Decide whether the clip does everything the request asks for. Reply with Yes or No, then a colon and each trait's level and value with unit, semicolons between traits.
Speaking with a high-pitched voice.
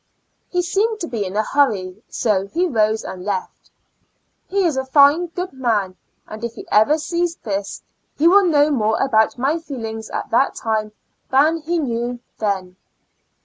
Yes: high, 245 Hz